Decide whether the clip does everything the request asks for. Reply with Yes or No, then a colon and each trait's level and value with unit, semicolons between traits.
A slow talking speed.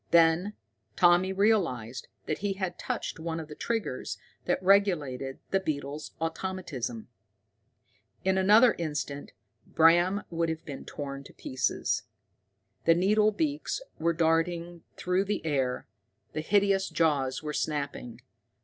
Yes: slow, 125 wpm